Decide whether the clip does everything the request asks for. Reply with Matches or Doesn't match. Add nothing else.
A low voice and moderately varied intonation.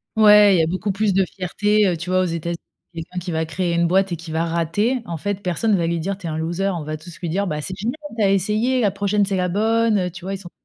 Doesn't match